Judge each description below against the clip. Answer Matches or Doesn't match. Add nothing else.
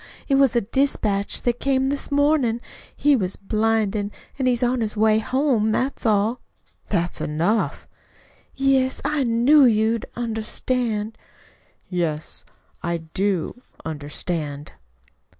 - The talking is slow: Matches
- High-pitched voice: Matches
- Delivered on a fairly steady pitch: Doesn't match